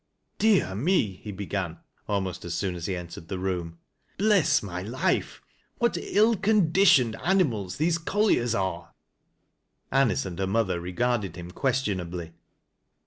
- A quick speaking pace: No, average, 150 wpm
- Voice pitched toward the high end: No, low, 100 Hz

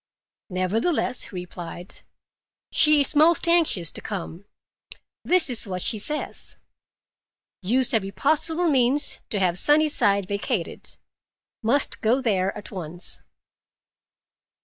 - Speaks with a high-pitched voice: Yes, high, 225 Hz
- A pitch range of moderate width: No, wide, 7.9 semitones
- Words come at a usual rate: No, slow, 110 wpm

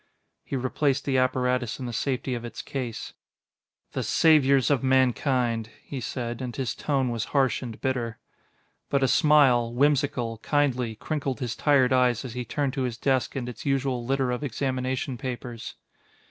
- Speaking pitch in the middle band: No, low, 130 Hz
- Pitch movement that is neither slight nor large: No, narrow, 2.2 semitones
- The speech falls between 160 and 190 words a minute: Yes, average, 165 wpm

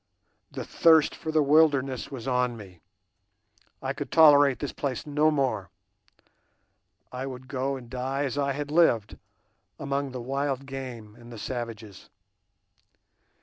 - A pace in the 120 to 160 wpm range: Yes, average, 140 wpm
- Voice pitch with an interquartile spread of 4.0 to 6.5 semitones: No, narrow, 2.4 semitones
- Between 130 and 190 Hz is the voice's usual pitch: Yes, low, 135 Hz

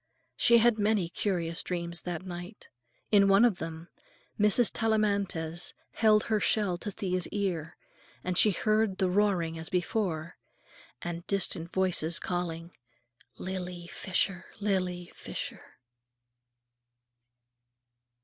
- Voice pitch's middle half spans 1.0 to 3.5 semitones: Yes, average, 3.1 semitones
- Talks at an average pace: No, slow, 110 wpm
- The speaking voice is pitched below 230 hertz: Yes, medium, 185 Hz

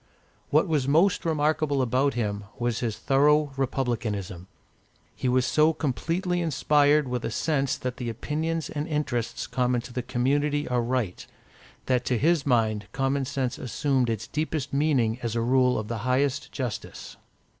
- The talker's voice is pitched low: Yes, low, 130 Hz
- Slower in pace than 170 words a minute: Yes, average, 155 wpm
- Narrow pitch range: No, average, 3.6 semitones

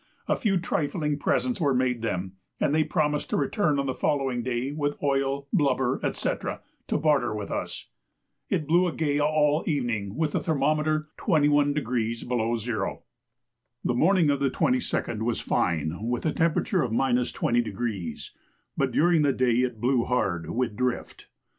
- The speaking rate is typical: Yes, average, 160 wpm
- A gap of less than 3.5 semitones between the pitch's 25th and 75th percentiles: No, average, 4.0 semitones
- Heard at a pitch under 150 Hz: Yes, low, 135 Hz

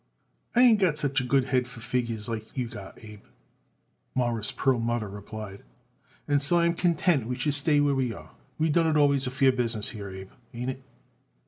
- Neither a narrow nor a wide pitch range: Yes, average, 4.2 semitones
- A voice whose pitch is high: No, low, 130 Hz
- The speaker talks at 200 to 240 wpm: Yes, fast, 205 wpm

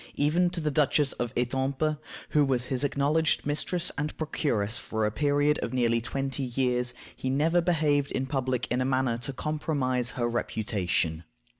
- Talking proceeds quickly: No, average, 165 wpm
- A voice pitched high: No, low, 135 Hz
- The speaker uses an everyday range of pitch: Yes, average, 3.4 semitones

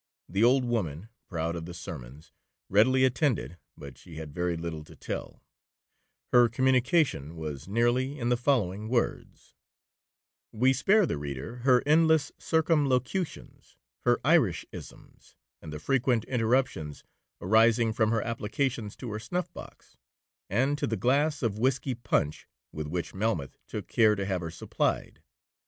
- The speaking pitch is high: No, low, 115 Hz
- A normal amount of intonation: No, wide, 7.1 semitones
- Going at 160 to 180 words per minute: No, average, 140 wpm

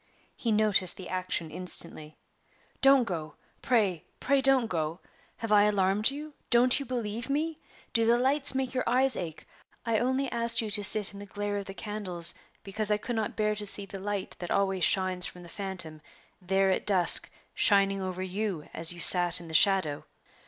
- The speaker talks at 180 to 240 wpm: Yes, average, 190 wpm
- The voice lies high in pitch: Yes, high, 205 Hz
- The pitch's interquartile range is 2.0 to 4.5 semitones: Yes, average, 4.0 semitones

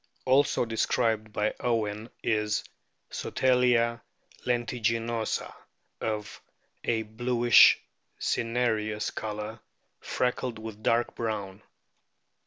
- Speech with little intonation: Yes, narrow, 1.9 semitones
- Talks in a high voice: No, low, 115 Hz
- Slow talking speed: Yes, slow, 75 wpm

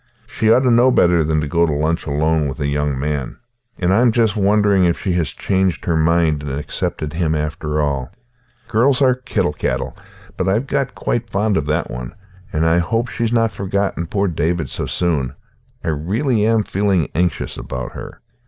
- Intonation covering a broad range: Yes, wide, 5.7 semitones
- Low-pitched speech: Yes, very low, 85 Hz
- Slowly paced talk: No, average, 195 wpm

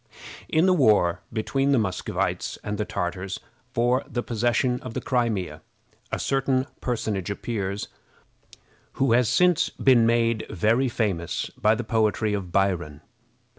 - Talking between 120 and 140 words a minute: Yes, slow, 135 wpm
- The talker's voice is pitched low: Yes, low, 115 Hz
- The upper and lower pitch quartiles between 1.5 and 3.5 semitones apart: No, average, 3.9 semitones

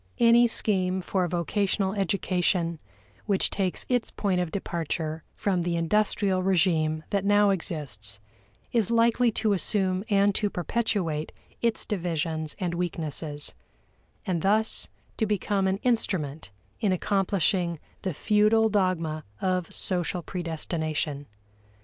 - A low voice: No, medium, 185 Hz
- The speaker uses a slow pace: Yes, slow, 120 wpm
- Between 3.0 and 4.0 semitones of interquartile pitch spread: Yes, average, 3.7 semitones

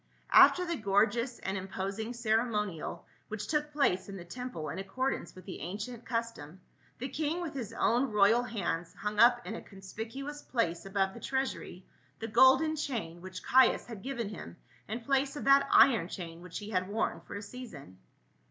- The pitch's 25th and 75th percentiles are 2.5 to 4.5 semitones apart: No, average, 5.1 semitones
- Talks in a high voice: Yes, high, 220 Hz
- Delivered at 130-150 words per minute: No, average, 180 wpm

